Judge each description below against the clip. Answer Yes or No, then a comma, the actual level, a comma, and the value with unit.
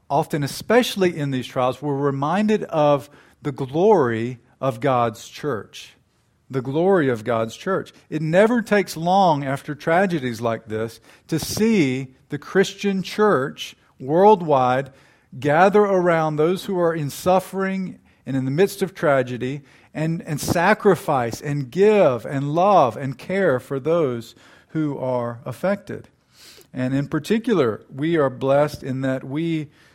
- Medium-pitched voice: Yes, medium, 150 Hz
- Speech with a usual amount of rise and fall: No, wide, 5.9 semitones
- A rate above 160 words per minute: No, slow, 135 wpm